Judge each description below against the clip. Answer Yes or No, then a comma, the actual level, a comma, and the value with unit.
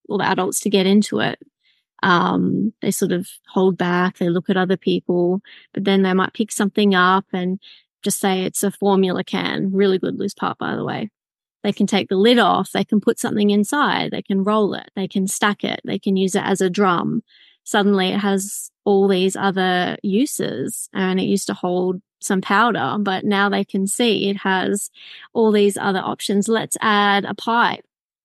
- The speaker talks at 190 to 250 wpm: Yes, average, 200 wpm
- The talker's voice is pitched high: Yes, high, 195 Hz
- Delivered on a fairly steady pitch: Yes, narrow, 1.5 semitones